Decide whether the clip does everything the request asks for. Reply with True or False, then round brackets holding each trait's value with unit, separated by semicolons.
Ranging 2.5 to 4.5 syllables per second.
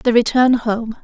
True (4.1 syllables/s)